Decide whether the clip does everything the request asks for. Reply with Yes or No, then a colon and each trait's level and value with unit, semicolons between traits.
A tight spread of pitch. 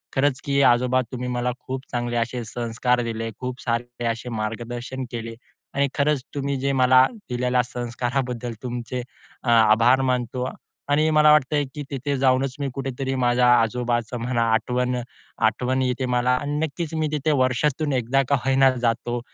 Yes: narrow, 2.0 semitones